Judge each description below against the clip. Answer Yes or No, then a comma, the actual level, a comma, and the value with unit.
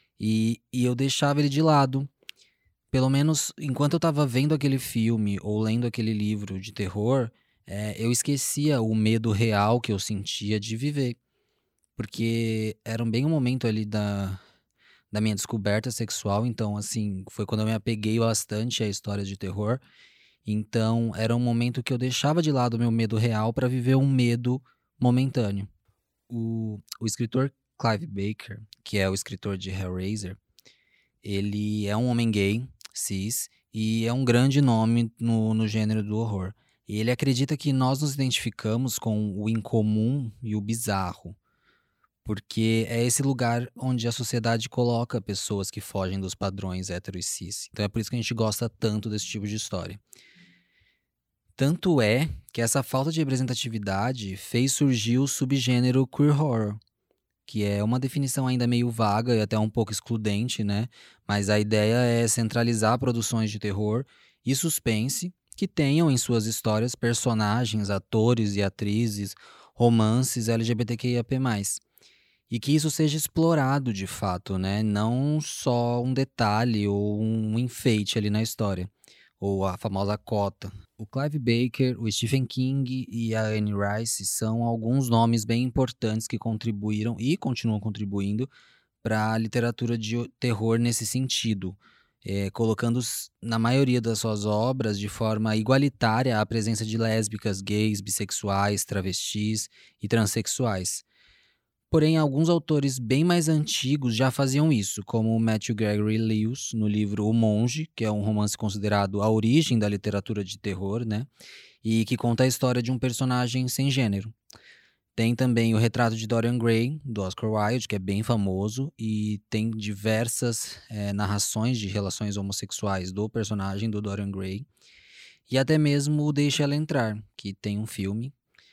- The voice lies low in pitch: Yes, low, 115 Hz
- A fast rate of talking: No, average, 155 wpm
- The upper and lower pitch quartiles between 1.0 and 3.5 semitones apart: Yes, average, 3.1 semitones